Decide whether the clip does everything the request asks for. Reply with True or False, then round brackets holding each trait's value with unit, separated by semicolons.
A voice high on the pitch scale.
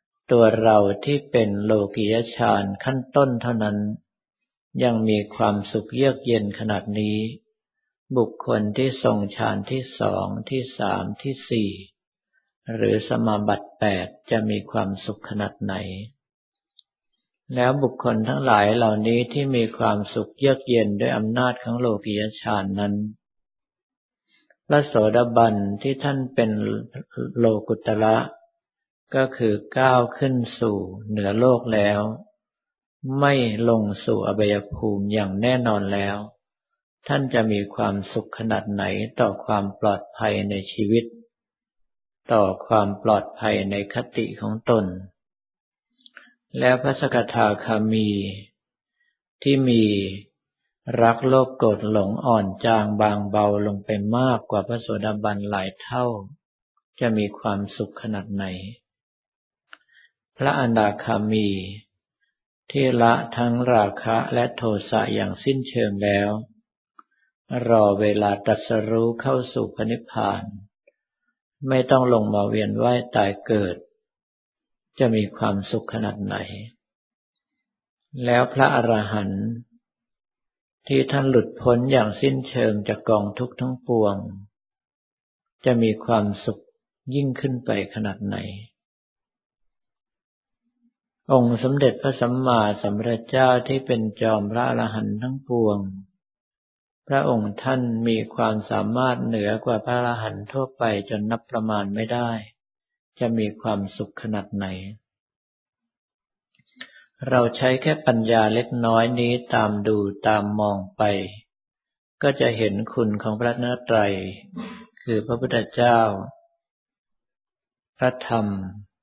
False (115 Hz)